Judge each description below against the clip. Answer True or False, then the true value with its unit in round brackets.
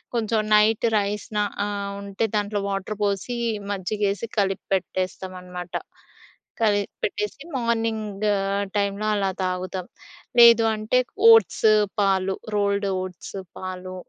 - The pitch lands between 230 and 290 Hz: False (200 Hz)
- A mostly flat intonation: True (2.0 semitones)